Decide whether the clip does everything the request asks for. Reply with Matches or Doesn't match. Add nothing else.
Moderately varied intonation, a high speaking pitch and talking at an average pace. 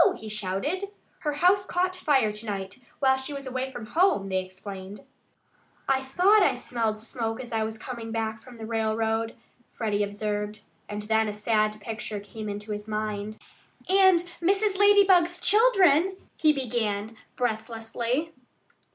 Doesn't match